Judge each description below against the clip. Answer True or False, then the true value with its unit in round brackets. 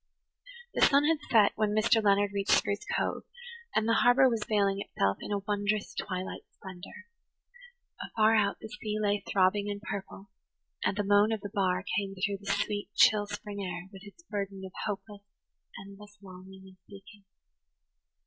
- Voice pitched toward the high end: True (205 Hz)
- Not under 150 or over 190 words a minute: True (170 wpm)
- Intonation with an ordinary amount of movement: False (1.4 semitones)